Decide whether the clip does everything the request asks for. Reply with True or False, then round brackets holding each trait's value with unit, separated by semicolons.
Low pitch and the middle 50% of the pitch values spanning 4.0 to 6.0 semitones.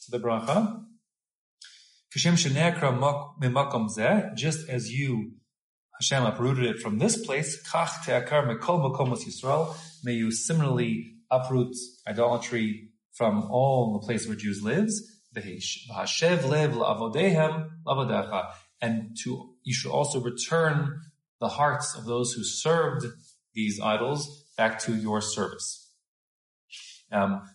True (125 Hz; 5.2 semitones)